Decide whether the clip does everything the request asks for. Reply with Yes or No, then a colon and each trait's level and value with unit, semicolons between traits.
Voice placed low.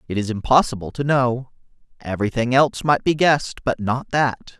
Yes: low, 125 Hz